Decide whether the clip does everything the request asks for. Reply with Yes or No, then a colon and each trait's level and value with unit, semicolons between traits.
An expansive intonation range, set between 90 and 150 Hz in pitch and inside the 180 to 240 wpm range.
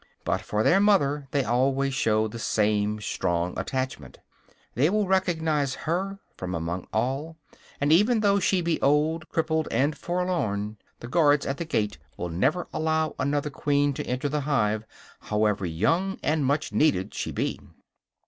No: wide, 6.9 semitones; medium, 140 Hz; average, 160 wpm